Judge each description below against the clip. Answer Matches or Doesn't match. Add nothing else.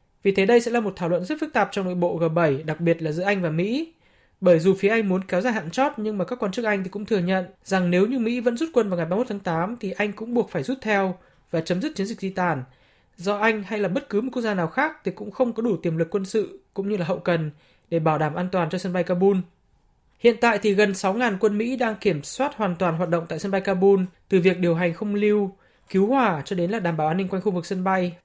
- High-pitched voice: Matches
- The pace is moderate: Doesn't match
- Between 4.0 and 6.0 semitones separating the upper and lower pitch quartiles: Doesn't match